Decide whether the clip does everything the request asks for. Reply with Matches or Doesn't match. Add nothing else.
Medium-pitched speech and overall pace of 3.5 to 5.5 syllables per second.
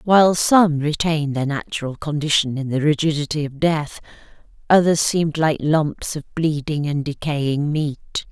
Matches